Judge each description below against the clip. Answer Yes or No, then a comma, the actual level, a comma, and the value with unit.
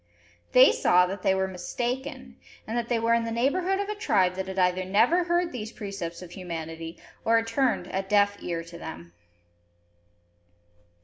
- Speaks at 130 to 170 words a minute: No, average, 180 wpm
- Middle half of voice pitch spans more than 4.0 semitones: Yes, average, 5.1 semitones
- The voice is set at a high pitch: Yes, high, 205 Hz